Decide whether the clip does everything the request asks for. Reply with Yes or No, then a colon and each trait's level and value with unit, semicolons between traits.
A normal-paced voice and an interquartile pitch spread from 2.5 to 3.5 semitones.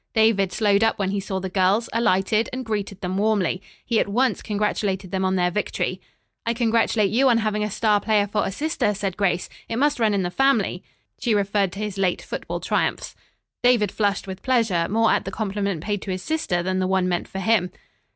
No: fast, 215 wpm; average, 2.8 semitones